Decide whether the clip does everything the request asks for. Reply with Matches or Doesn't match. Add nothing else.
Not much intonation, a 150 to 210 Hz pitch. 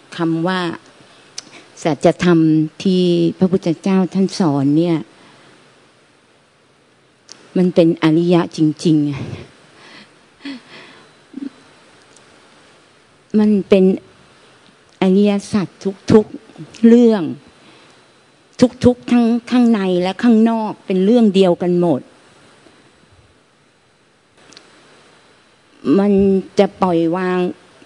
Doesn't match